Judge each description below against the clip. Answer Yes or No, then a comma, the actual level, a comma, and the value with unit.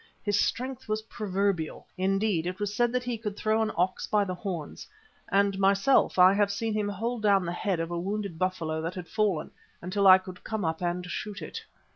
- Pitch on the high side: Yes, high, 195 Hz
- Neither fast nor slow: No, fast, 210 wpm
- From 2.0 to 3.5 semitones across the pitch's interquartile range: Yes, average, 2.8 semitones